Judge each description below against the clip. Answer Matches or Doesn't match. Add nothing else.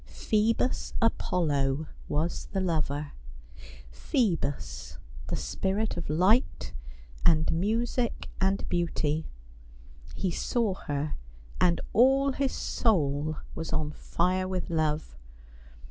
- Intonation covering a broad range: Matches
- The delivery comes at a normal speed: Doesn't match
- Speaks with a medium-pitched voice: Matches